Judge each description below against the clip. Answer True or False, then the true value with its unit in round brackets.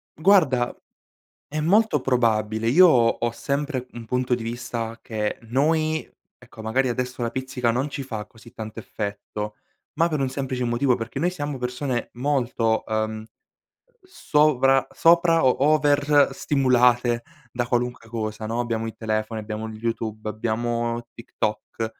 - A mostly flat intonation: False (3.6 semitones)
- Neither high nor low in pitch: False (120 Hz)